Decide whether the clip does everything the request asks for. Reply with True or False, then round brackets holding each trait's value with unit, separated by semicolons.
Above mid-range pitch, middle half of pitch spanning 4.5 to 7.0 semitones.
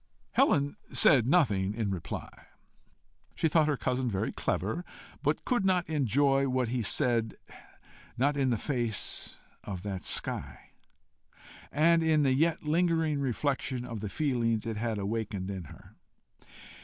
False (130 Hz; 5.4 semitones)